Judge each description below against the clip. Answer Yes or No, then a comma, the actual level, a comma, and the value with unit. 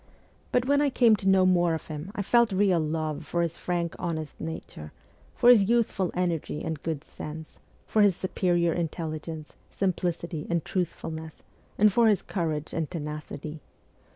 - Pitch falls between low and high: Yes, medium, 170 Hz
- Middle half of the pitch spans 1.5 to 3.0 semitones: No, average, 3.6 semitones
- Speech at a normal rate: Yes, average, 160 wpm